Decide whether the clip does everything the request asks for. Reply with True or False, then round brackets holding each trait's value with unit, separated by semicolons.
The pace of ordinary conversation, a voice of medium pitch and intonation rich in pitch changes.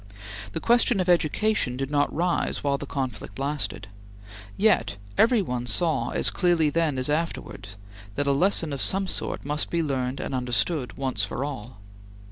False (165 wpm; 145 Hz; 5.0 semitones)